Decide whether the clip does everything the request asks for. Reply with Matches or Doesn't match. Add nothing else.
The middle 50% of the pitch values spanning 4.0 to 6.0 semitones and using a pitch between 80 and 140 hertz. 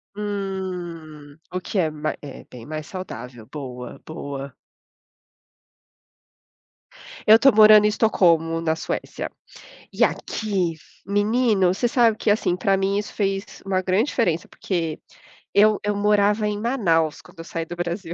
Doesn't match